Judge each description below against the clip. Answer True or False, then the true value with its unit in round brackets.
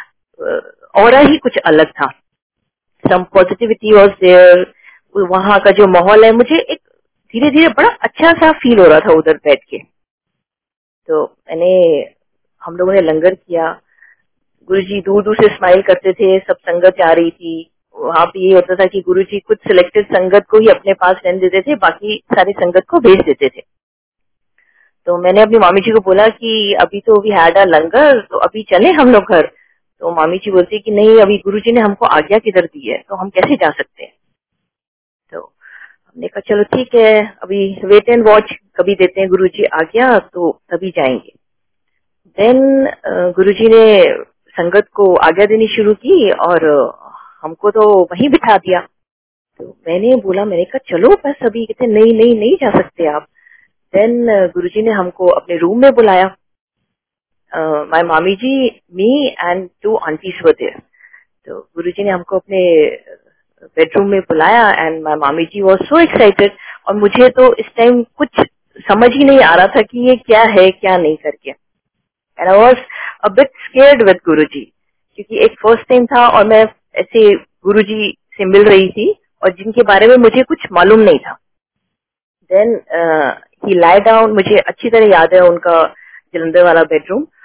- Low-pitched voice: False (210 Hz)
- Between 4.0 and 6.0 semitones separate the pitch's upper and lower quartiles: True (5.6 semitones)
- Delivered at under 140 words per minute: False (175 wpm)